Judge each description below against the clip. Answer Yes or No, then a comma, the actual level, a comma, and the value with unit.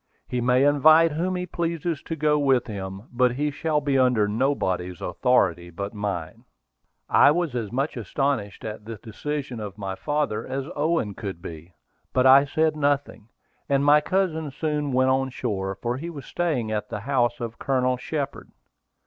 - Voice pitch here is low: Yes, low, 130 Hz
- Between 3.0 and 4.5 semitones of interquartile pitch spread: No, wide, 5.6 semitones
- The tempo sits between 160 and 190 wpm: Yes, average, 175 wpm